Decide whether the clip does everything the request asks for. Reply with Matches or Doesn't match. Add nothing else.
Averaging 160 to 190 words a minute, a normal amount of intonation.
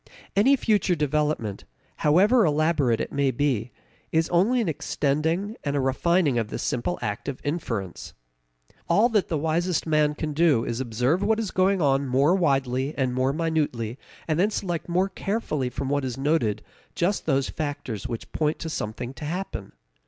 Matches